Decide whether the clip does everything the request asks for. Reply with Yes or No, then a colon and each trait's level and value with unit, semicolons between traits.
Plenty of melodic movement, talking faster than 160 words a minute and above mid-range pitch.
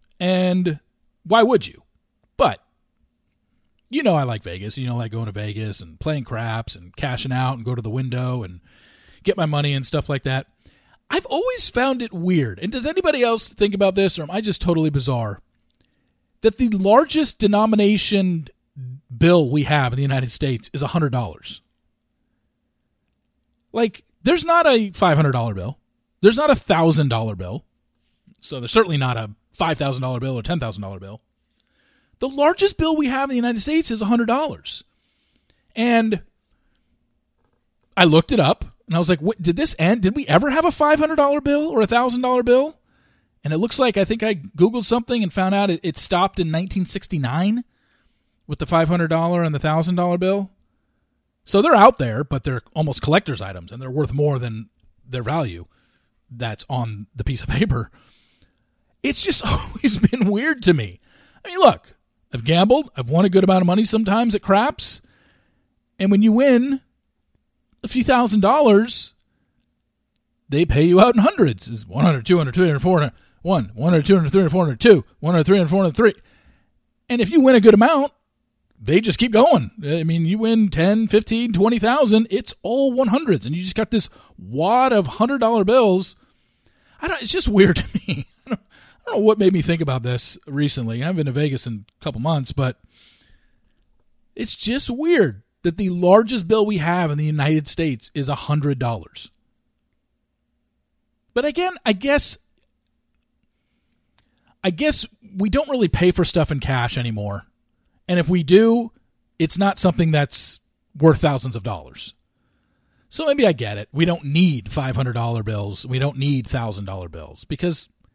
No: wide, 8.7 semitones; average, 175 wpm; medium, 175 Hz